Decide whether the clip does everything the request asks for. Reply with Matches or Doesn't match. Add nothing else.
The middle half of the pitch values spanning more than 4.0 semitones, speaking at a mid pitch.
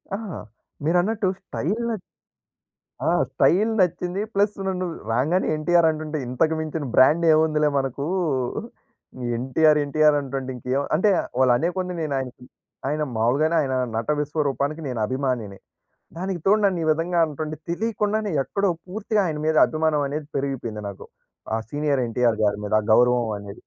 Matches